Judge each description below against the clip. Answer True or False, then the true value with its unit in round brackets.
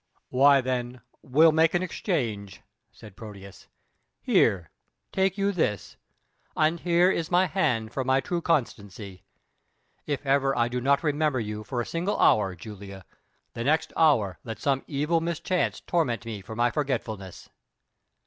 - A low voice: True (130 Hz)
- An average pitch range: False (6.8 semitones)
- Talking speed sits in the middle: True (150 wpm)